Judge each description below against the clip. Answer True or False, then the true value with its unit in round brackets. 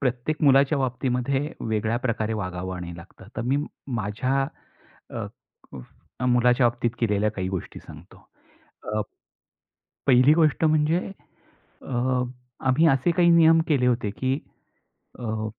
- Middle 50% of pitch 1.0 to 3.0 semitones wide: False (4.1 semitones)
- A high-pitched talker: False (125 Hz)